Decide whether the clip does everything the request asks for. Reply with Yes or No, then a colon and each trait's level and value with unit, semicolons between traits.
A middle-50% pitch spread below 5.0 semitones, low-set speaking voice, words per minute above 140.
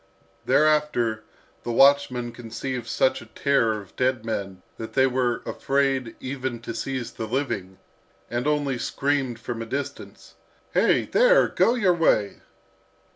No: average, 3.5 semitones; low, 125 Hz; slow, 135 wpm